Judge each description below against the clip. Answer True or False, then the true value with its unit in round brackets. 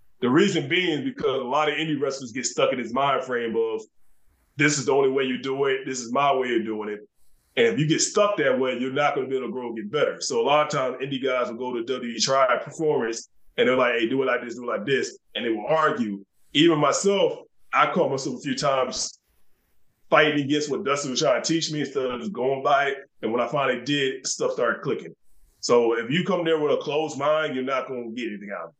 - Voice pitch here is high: False (140 Hz)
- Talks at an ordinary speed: False (265 wpm)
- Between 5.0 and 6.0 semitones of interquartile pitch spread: False (3.9 semitones)